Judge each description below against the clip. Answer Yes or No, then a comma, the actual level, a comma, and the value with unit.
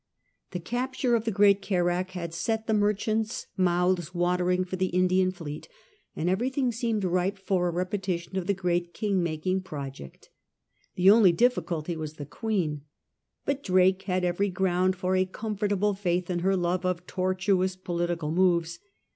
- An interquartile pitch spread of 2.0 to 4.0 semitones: Yes, narrow, 2.4 semitones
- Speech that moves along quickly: No, average, 160 wpm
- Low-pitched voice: No, medium, 185 Hz